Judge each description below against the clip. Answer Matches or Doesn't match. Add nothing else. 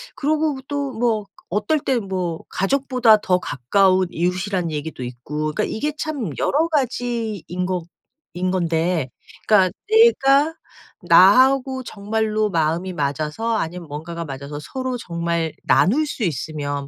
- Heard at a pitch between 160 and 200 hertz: Matches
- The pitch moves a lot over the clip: Matches